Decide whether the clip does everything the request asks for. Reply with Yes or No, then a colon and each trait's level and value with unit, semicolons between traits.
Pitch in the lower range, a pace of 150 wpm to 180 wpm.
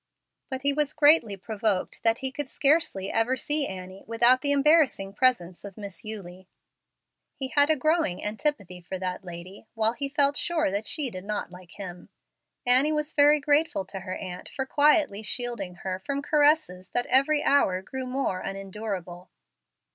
No: high, 230 Hz; average, 170 wpm